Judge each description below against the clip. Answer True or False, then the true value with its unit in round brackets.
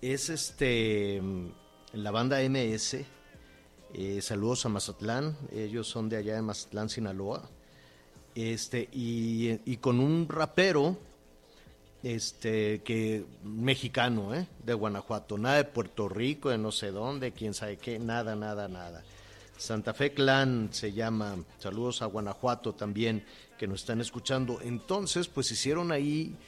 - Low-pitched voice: True (115 Hz)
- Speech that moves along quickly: False (135 wpm)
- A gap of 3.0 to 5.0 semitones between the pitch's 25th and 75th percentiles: True (3.4 semitones)